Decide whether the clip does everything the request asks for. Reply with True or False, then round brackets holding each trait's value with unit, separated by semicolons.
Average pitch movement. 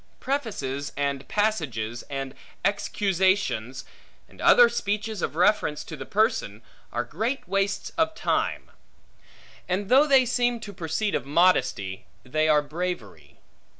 False (7.7 semitones)